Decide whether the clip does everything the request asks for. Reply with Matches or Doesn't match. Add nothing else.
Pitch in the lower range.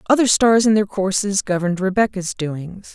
Doesn't match